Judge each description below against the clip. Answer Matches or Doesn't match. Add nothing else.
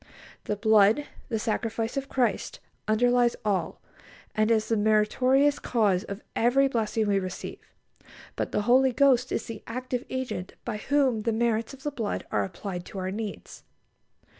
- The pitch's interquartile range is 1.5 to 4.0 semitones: Matches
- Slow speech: Doesn't match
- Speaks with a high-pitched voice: Matches